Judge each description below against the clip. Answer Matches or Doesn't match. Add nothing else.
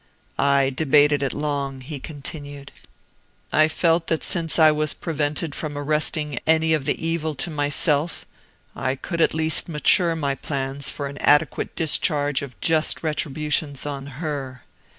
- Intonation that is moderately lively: Doesn't match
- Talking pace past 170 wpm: Doesn't match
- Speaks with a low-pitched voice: Doesn't match